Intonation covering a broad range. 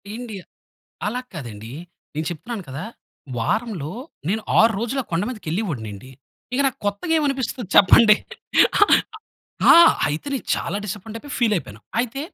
Yes: wide, 7.3 semitones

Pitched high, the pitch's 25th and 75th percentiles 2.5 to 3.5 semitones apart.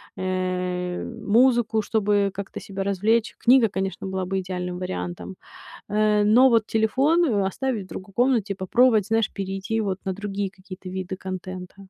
Yes: high, 200 Hz; average, 3.1 semitones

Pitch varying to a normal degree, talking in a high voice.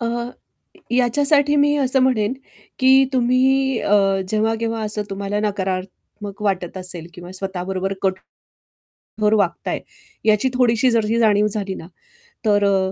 Yes: average, 4.2 semitones; high, 210 Hz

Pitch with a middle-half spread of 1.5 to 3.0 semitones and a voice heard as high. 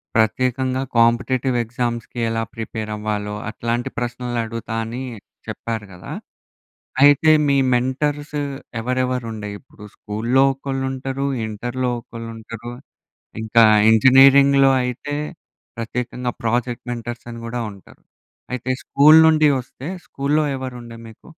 No: narrow, 2.4 semitones; low, 120 Hz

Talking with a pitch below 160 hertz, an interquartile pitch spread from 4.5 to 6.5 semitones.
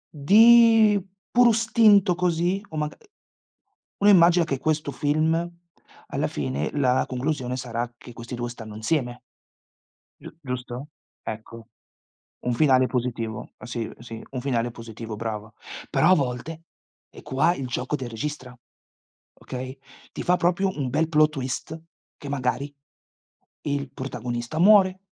Yes: low, 135 Hz; average, 5.2 semitones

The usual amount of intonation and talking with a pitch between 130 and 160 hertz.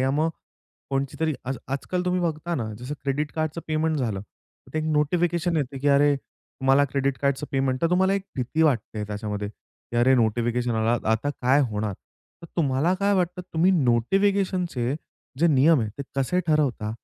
Yes: average, 5.0 semitones; medium, 140 Hz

